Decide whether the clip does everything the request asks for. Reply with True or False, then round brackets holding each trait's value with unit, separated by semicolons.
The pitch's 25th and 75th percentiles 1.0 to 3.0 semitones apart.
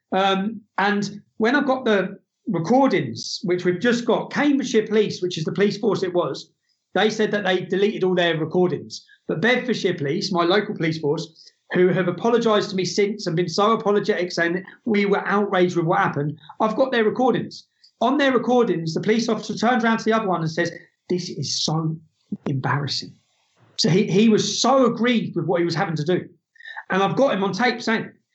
False (3.8 semitones)